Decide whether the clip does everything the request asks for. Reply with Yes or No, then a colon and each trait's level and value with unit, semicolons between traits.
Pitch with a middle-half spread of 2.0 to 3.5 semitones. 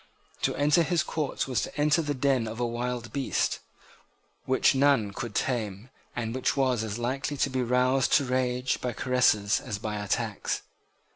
Yes: average, 2.9 semitones